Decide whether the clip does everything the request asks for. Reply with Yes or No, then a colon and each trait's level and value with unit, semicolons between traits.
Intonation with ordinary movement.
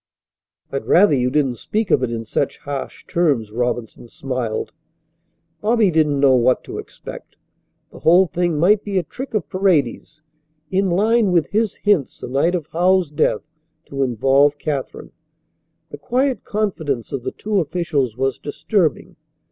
No: wide, 6.0 semitones